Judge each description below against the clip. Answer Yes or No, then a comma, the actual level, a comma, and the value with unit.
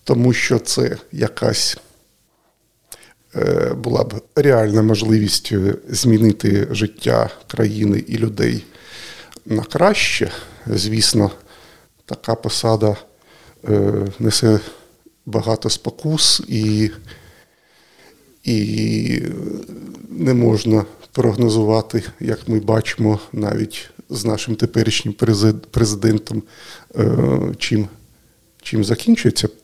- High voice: No, low, 110 Hz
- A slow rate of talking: Yes, slow, 75 wpm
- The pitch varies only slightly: Yes, narrow, 1.2 semitones